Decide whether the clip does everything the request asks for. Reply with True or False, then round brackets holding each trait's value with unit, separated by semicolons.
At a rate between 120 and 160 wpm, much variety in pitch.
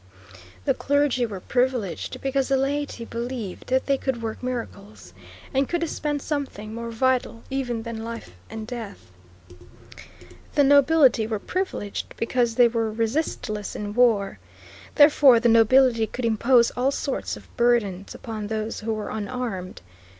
False (145 wpm; 3.2 semitones)